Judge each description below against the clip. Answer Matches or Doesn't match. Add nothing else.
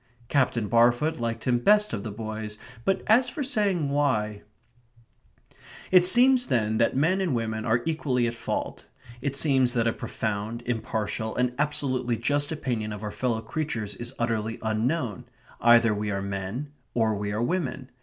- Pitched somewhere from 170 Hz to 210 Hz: Doesn't match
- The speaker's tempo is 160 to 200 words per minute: Matches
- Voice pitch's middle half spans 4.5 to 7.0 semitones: Matches